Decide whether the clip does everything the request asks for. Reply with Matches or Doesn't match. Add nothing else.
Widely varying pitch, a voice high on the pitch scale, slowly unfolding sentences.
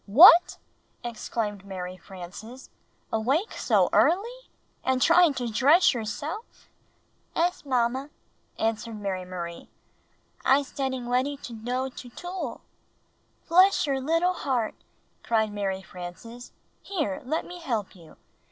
Matches